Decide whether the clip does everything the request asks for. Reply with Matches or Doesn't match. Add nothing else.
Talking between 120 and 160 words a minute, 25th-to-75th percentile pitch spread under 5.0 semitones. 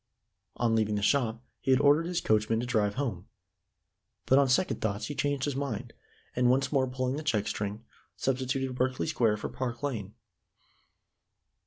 Doesn't match